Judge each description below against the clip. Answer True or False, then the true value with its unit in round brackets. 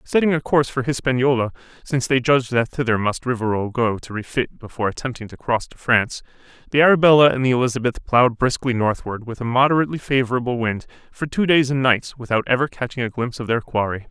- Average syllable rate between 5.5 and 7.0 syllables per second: True (6.5 syllables/s)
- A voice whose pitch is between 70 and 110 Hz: False (125 Hz)